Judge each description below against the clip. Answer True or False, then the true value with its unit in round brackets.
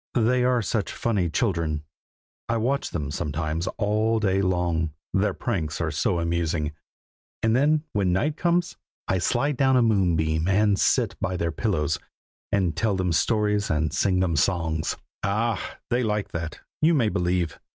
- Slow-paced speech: False (160 wpm)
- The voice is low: True (95 Hz)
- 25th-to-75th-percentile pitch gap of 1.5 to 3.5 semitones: False (5.3 semitones)